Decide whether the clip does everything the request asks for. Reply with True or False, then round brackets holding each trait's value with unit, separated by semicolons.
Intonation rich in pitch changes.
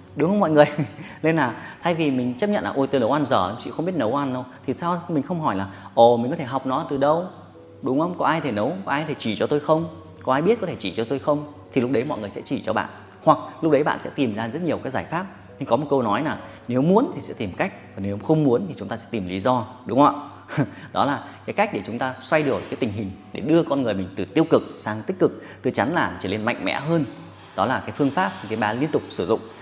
True (6.0 semitones)